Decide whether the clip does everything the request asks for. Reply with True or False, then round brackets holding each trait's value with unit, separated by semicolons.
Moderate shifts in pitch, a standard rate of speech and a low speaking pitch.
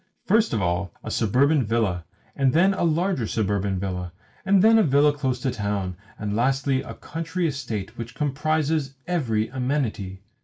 False (7.0 semitones; 165 wpm; 130 Hz)